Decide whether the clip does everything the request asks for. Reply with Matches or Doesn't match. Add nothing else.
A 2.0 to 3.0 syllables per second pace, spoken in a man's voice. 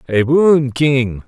Matches